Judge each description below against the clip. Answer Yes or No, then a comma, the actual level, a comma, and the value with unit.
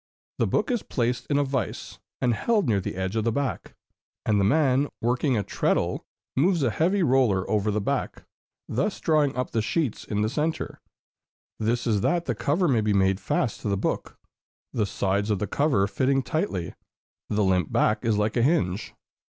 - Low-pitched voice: Yes, low, 115 Hz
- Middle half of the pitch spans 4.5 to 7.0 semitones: Yes, wide, 5.5 semitones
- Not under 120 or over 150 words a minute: No, average, 190 wpm